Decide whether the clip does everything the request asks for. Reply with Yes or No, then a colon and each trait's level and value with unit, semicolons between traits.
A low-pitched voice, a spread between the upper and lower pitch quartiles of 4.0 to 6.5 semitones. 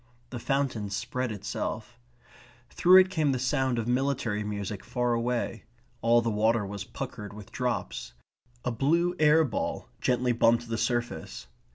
No: low, 120 Hz; average, 3.4 semitones